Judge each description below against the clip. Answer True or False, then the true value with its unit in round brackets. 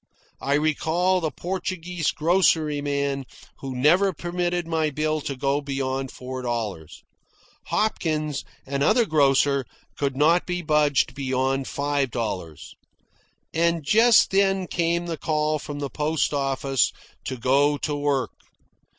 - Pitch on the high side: False (145 Hz)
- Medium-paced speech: False (125 wpm)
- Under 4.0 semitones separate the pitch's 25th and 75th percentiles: True (3.6 semitones)